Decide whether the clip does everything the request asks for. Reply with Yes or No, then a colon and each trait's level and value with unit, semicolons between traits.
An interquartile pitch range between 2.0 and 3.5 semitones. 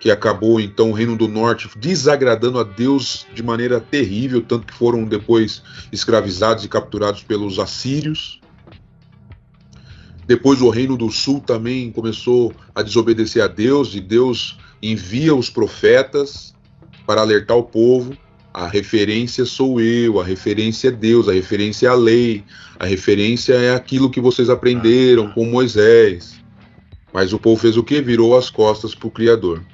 Yes: narrow, 2.5 semitones